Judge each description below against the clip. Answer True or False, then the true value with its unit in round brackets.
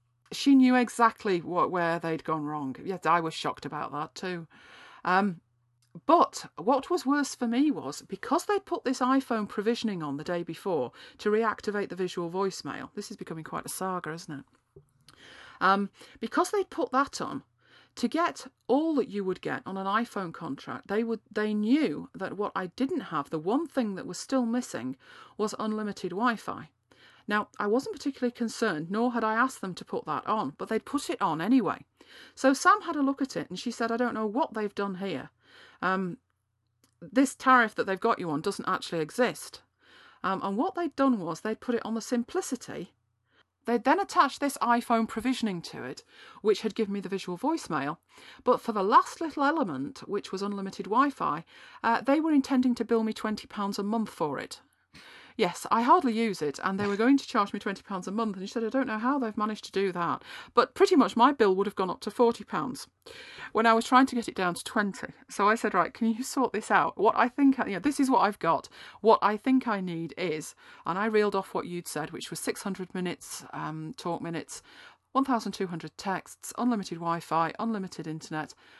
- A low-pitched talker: False (220 Hz)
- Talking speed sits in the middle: False (215 wpm)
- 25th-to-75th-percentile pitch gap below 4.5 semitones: False (5.6 semitones)